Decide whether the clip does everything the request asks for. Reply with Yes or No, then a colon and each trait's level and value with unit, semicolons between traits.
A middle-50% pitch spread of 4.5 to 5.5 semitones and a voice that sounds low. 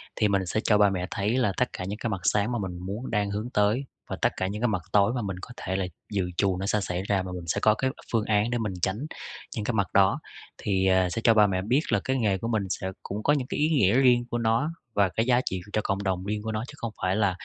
No: average, 3.2 semitones; low, 105 Hz